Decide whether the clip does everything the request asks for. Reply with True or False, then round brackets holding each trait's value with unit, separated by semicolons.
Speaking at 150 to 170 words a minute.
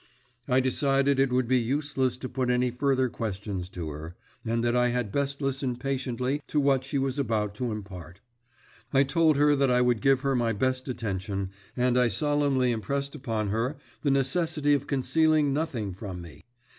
False (185 wpm)